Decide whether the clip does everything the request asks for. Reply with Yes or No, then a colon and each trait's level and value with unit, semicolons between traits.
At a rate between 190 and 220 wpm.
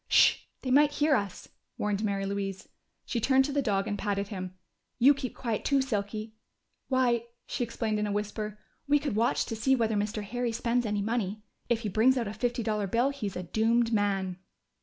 Yes: average, 200 wpm